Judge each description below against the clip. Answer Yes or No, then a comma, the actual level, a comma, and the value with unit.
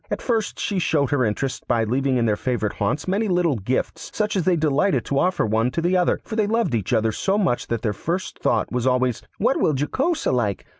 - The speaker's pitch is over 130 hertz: Yes, medium, 140 Hz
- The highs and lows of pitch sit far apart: Yes, wide, 7.9 semitones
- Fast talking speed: Yes, fast, 235 wpm